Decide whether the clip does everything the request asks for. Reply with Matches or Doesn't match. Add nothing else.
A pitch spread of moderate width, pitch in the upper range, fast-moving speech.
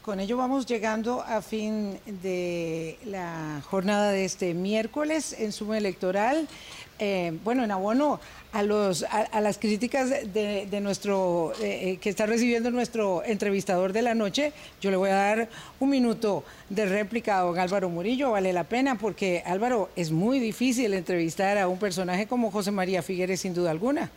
Doesn't match